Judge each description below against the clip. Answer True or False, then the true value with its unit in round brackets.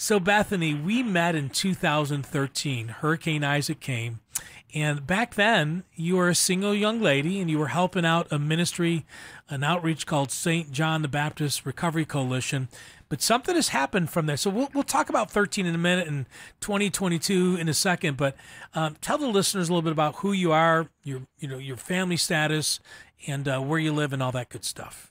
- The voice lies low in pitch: False (160 Hz)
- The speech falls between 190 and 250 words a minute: True (200 wpm)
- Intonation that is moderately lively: True (4.2 semitones)